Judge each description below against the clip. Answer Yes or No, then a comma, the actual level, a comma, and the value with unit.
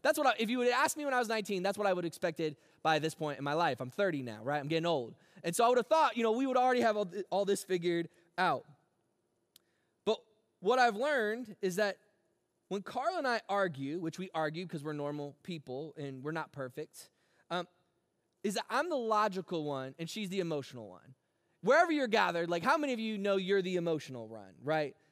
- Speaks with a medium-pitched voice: Yes, medium, 180 Hz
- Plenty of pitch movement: Yes, wide, 6.0 semitones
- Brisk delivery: Yes, fast, 230 wpm